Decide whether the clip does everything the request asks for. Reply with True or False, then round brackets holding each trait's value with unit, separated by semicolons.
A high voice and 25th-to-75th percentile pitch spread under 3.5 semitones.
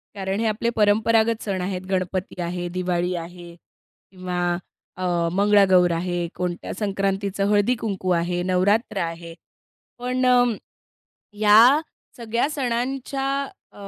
False (195 Hz; 3.8 semitones)